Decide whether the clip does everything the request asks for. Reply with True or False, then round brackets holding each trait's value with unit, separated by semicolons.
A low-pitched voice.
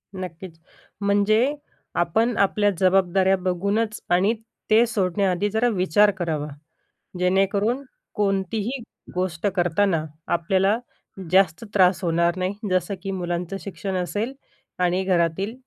False (190 Hz)